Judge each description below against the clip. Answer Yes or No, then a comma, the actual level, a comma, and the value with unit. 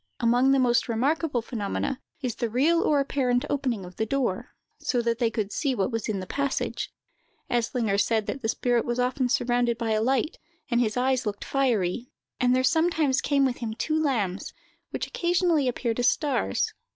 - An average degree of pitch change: Yes, average, 3.2 semitones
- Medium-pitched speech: No, high, 245 Hz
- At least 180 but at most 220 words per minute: Yes, average, 190 wpm